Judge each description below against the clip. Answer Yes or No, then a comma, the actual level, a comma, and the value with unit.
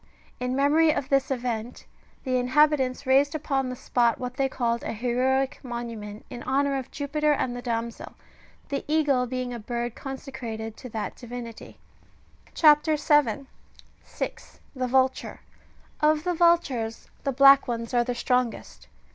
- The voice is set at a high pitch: Yes, very high, 255 Hz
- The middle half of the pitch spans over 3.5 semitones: No, average, 2.8 semitones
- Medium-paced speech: Yes, average, 145 wpm